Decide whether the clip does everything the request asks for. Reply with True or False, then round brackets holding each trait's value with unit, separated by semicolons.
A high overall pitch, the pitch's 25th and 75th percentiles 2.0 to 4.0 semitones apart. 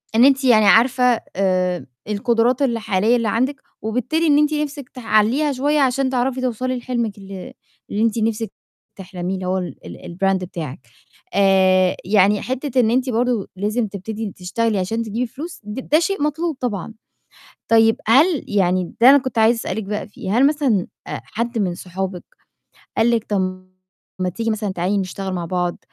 False (225 Hz; 4.8 semitones)